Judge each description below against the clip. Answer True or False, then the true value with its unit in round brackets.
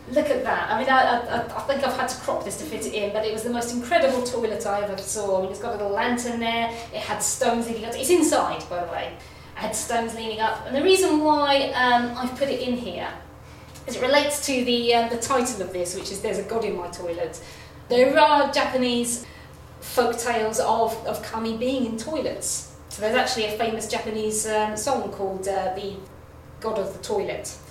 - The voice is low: False (235 Hz)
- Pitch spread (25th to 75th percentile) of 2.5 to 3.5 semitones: True (3.0 semitones)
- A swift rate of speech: True (225 wpm)